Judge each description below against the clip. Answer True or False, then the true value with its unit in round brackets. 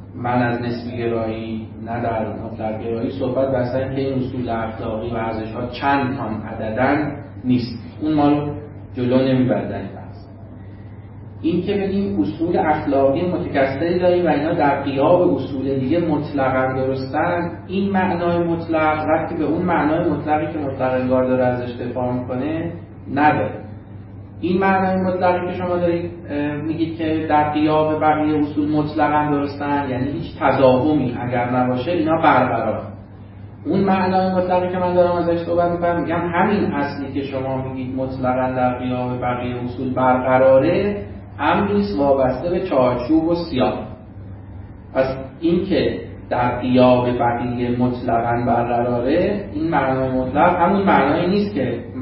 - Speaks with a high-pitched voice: False (130 Hz)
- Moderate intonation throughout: True (4.6 semitones)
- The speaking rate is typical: True (135 wpm)